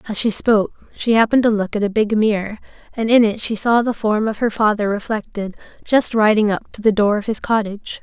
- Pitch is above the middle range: Yes, high, 215 Hz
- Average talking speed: No, fast, 230 wpm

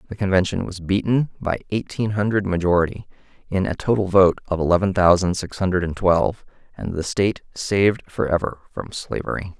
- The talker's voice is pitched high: No, very low, 95 Hz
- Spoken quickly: No, average, 155 wpm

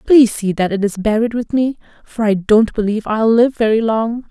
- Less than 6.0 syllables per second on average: Yes, 5.3 syllables/s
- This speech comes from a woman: Yes, female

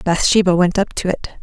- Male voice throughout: No, female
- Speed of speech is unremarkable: No, fast, 210 wpm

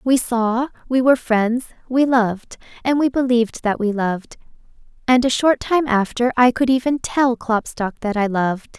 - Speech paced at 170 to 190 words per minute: Yes, average, 180 wpm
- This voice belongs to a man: No, female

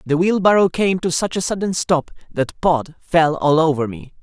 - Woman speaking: No, male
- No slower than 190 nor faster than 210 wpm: Yes, average, 200 wpm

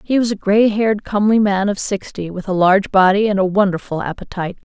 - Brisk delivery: Yes, fast, 215 wpm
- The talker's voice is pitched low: No, high, 200 Hz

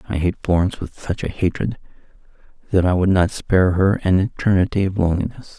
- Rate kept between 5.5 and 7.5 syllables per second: Yes, 6.1 syllables/s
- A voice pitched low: Yes, very low, 95 Hz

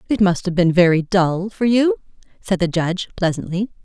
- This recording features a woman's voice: Yes, female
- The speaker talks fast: No, average, 190 wpm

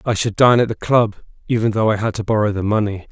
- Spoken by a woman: No, male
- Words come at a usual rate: No, fast, 270 wpm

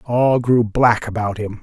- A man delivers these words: Yes, male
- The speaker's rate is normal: Yes, average, 185 wpm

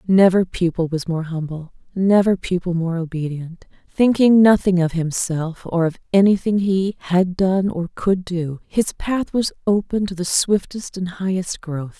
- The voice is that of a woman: Yes, female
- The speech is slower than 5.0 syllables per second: Yes, 4.3 syllables/s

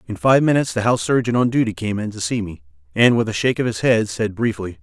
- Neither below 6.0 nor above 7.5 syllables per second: Yes, 6.7 syllables/s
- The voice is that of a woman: No, male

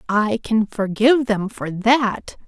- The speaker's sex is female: Yes, female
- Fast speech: No, average, 145 wpm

